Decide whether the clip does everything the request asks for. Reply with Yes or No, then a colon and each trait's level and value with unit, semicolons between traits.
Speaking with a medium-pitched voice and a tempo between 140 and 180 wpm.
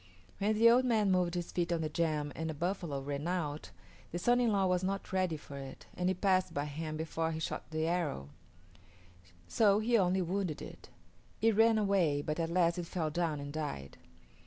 No: medium, 175 Hz; fast, 205 wpm